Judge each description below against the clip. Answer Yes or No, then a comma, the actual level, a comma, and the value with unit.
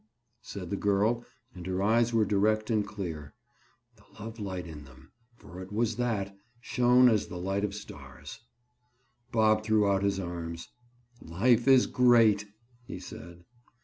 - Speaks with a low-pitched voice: Yes, low, 100 Hz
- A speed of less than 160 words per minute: Yes, average, 145 wpm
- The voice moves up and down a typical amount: Yes, average, 3.9 semitones